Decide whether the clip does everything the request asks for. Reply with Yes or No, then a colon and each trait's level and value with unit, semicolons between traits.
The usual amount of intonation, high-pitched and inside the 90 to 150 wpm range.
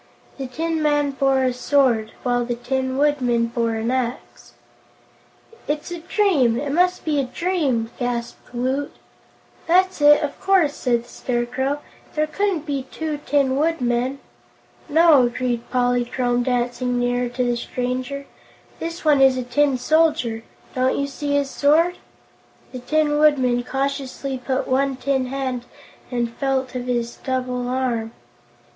Yes: average, 3.0 semitones; very high, 260 Hz; average, 145 wpm